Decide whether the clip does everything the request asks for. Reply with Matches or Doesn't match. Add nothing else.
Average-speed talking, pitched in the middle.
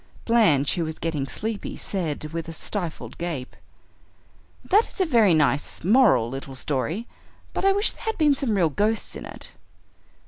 Matches